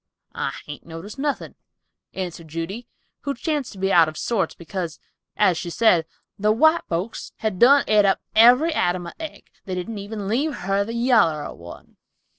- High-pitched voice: Yes, high, 200 Hz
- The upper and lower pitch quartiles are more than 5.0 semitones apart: Yes, wide, 5.5 semitones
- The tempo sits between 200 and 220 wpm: No, average, 180 wpm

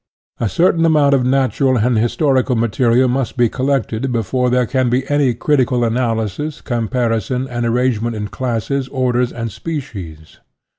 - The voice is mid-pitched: No, low, 125 Hz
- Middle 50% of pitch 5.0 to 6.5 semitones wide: No, narrow, 2.5 semitones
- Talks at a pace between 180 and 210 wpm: No, average, 150 wpm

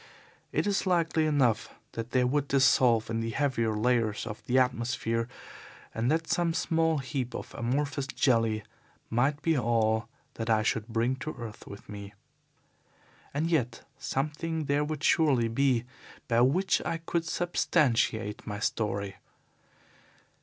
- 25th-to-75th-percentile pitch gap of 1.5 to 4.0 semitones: No, average, 4.6 semitones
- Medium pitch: No, low, 125 Hz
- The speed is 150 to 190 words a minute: No, average, 140 wpm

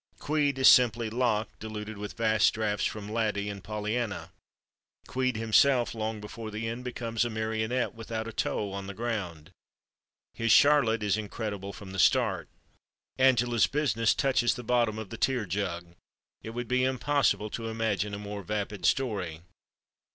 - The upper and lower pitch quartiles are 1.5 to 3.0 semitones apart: Yes, average, 2.7 semitones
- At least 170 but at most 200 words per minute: No, average, 160 wpm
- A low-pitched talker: Yes, low, 110 Hz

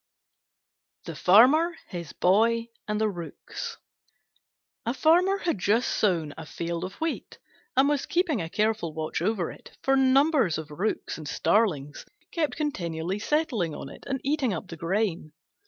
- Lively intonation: Yes, wide, 8.6 semitones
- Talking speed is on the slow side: No, average, 155 wpm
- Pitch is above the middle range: Yes, high, 215 Hz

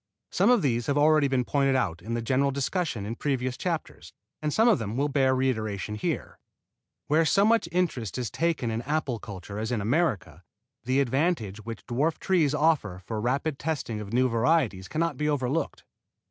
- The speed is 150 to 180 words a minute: No, average, 190 wpm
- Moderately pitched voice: No, low, 130 Hz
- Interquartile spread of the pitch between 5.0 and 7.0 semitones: Yes, wide, 5.4 semitones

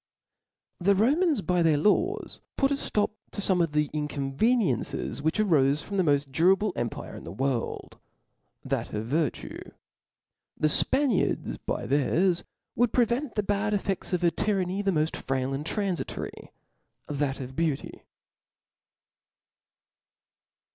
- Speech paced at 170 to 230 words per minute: No, slow, 135 wpm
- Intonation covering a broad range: Yes, wide, 6.1 semitones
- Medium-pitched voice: Yes, medium, 180 Hz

